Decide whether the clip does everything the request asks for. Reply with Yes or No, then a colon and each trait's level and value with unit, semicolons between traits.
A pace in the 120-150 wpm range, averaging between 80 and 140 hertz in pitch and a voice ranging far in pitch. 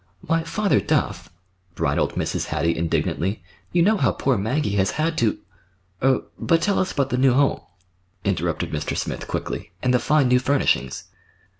No: average, 160 wpm; low, 135 Hz; wide, 7.7 semitones